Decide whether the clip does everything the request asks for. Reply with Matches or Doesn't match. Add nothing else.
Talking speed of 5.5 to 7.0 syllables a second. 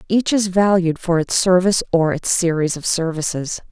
Doesn't match